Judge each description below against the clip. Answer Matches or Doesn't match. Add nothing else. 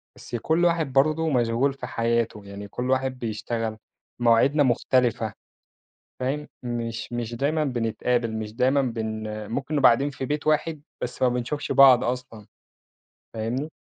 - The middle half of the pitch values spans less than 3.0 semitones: Doesn't match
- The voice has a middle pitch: Doesn't match